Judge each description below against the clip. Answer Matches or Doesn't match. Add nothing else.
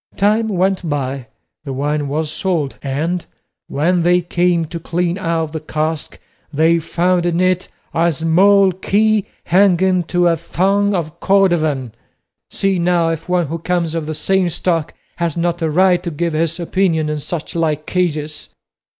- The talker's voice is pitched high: Doesn't match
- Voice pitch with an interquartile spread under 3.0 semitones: Matches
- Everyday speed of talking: Matches